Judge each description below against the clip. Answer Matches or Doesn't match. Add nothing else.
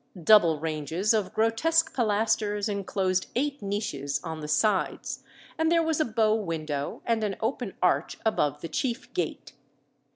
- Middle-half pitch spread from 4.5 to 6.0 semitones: Matches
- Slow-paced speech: Doesn't match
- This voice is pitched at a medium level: Doesn't match